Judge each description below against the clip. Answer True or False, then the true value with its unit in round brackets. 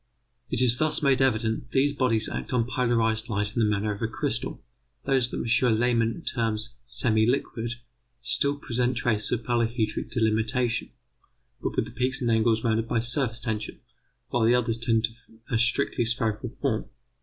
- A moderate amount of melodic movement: False (1.9 semitones)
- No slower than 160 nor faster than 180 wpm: True (175 wpm)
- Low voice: True (115 Hz)